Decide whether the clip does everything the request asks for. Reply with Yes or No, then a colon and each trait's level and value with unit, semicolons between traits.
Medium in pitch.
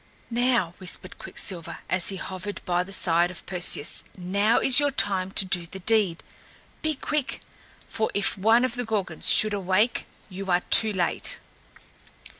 No: high, 195 Hz